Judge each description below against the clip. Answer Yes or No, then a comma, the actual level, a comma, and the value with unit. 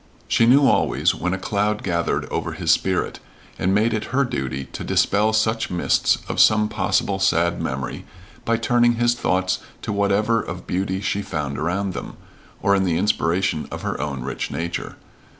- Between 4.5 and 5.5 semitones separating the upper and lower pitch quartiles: No, average, 4.0 semitones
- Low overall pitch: Yes, low, 100 Hz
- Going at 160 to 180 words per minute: Yes, average, 175 wpm